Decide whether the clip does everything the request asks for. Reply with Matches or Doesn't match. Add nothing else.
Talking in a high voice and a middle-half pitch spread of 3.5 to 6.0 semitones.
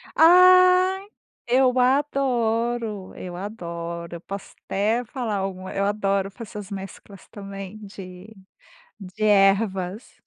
Matches